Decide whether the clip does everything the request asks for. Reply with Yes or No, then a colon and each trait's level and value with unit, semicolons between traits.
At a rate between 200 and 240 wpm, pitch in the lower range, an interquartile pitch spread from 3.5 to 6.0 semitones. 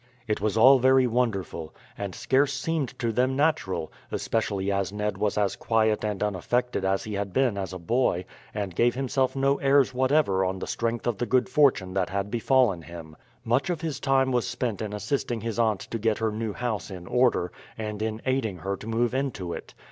Yes: fast, 205 wpm; low, 110 Hz; average, 4.7 semitones